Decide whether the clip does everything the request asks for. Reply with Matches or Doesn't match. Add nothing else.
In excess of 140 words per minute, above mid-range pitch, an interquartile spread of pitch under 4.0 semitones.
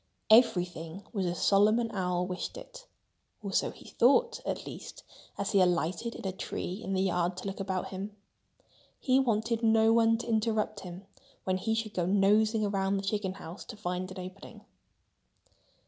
Matches